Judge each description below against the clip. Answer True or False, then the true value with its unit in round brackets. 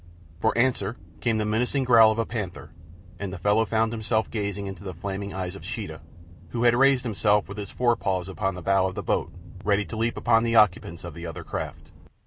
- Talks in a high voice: False (105 Hz)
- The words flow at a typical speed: False (220 wpm)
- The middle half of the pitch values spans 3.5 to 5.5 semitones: False (3.0 semitones)